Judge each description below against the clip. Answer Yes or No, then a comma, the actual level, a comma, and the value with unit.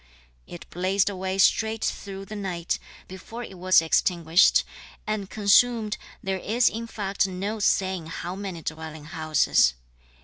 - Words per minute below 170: Yes, slow, 135 wpm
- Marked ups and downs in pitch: No, average, 3.2 semitones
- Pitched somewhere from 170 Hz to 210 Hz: Yes, high, 190 Hz